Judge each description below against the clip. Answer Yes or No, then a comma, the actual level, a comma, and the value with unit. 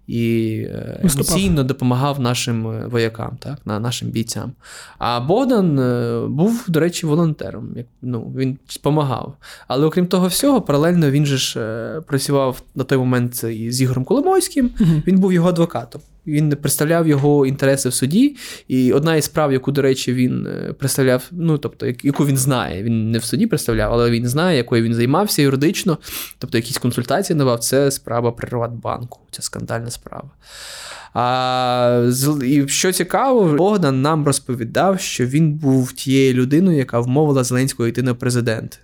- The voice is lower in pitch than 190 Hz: Yes, low, 135 Hz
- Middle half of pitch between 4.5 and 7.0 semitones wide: No, average, 4.1 semitones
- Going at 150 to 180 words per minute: Yes, fast, 155 wpm